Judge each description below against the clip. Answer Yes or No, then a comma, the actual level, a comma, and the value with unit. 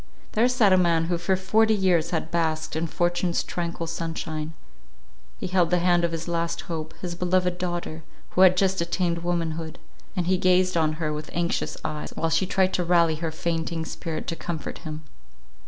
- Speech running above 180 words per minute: Yes, average, 190 wpm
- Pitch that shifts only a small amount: Yes, narrow, 1.8 semitones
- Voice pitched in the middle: Yes, medium, 170 Hz